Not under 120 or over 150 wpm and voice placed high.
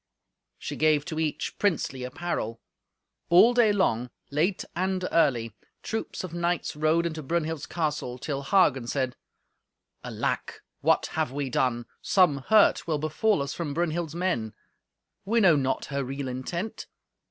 No: average, 140 wpm; medium, 155 Hz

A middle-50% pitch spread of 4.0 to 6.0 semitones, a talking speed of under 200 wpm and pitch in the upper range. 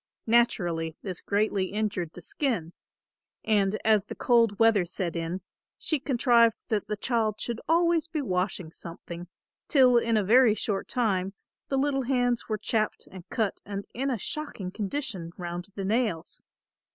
Yes: average, 4.5 semitones; average, 155 wpm; high, 215 Hz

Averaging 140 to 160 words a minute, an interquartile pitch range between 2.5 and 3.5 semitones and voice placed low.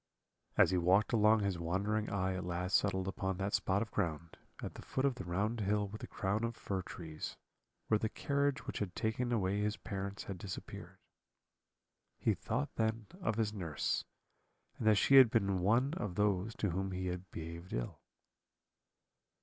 No: average, 180 wpm; average, 3.0 semitones; low, 100 Hz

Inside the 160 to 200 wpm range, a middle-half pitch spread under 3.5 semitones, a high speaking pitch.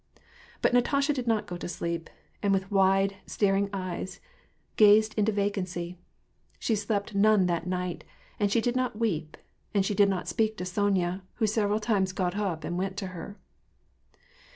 Yes: average, 175 wpm; average, 2.8 semitones; high, 200 Hz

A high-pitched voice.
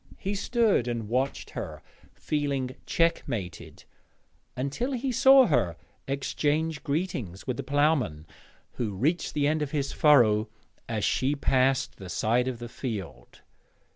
No: low, 135 Hz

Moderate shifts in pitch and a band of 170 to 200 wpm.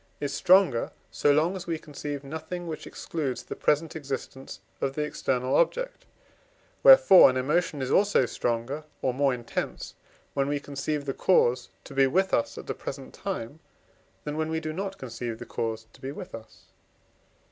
Yes: average, 3.7 semitones; average, 175 wpm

